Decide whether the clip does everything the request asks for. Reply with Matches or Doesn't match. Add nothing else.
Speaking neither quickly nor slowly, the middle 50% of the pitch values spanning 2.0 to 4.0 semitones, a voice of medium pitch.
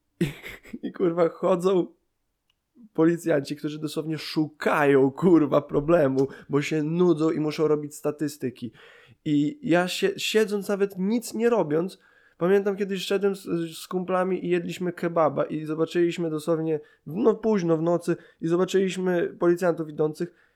Matches